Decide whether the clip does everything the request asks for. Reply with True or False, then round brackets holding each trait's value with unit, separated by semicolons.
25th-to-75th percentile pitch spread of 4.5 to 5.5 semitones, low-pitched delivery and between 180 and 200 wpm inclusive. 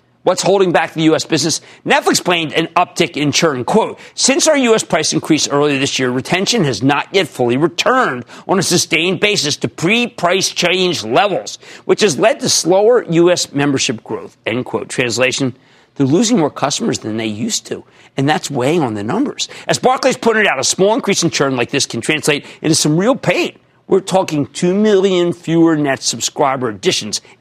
False (4.9 semitones; 165 Hz; 190 wpm)